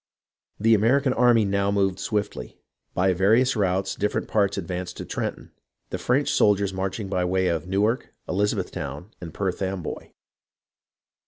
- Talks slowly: No, average, 145 wpm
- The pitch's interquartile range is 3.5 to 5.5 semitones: No, narrow, 2.4 semitones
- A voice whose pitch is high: No, low, 100 Hz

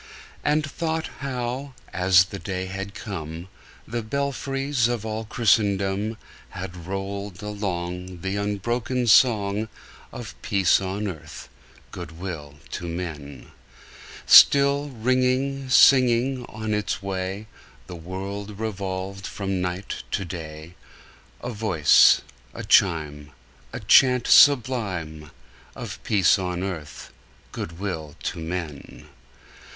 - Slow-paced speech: Yes, slow, 110 wpm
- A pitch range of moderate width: Yes, average, 4.8 semitones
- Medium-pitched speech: No, low, 100 Hz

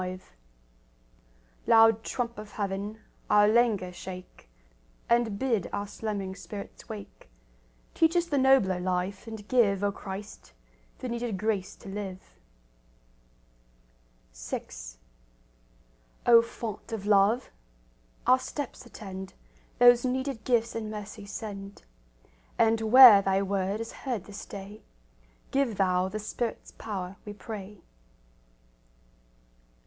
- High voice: Yes, high, 210 Hz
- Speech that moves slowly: Yes, slow, 115 wpm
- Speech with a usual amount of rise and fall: Yes, average, 3.0 semitones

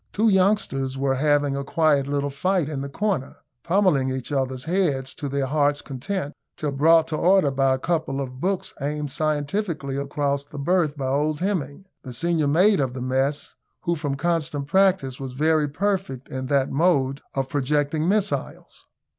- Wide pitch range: No, average, 3.7 semitones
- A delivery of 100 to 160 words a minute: No, average, 170 wpm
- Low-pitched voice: No, medium, 145 Hz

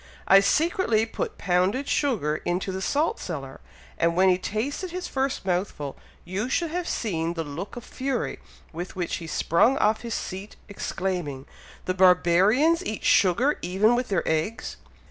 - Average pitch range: No, wide, 6.6 semitones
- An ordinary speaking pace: Yes, average, 160 wpm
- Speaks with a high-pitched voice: Yes, high, 195 Hz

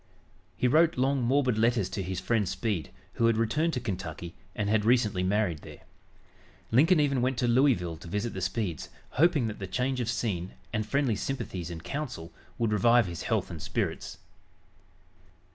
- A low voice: Yes, low, 115 Hz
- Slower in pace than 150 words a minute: No, average, 175 wpm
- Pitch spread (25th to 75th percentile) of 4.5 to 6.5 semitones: Yes, average, 5.1 semitones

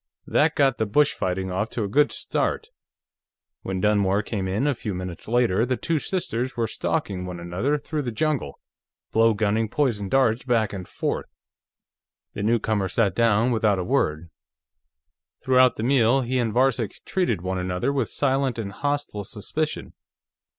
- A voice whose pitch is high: No, low, 115 Hz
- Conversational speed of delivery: Yes, average, 165 wpm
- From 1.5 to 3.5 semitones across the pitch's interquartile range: No, average, 5.1 semitones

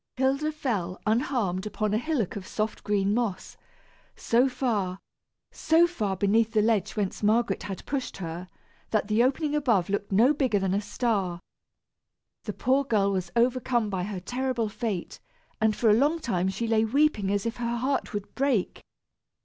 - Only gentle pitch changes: No, average, 4.3 semitones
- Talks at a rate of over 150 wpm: Yes, average, 170 wpm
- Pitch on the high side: Yes, high, 220 Hz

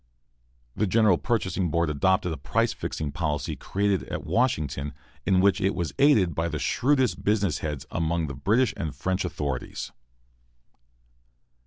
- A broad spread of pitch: No, average, 5.0 semitones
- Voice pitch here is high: No, very low, 90 Hz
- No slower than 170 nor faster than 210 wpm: No, average, 145 wpm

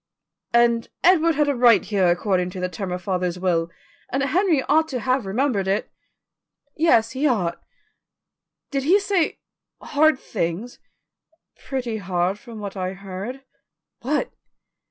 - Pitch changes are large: Yes, wide, 6.7 semitones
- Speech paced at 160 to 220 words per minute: No, average, 140 wpm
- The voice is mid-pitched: No, high, 230 Hz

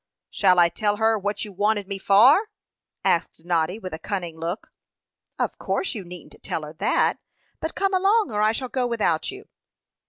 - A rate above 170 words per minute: Yes, average, 185 wpm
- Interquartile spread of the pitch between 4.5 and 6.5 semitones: Yes, average, 5.1 semitones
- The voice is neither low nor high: No, high, 205 Hz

